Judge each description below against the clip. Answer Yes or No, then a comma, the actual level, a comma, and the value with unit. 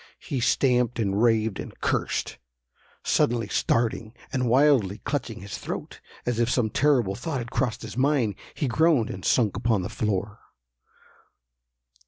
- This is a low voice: Yes, low, 120 Hz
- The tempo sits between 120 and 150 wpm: Yes, average, 145 wpm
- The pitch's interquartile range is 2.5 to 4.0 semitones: Yes, average, 3.2 semitones